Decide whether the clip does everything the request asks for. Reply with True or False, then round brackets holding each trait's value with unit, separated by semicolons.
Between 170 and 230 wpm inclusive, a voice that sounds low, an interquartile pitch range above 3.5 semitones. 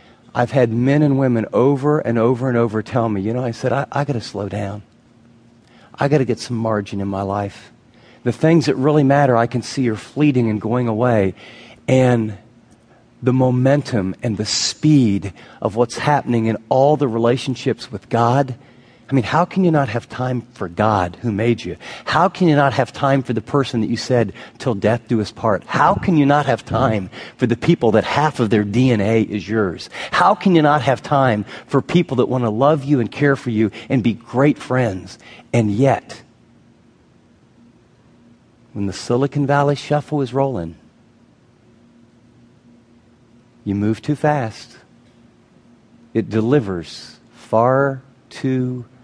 False (175 wpm; 120 Hz; 3.2 semitones)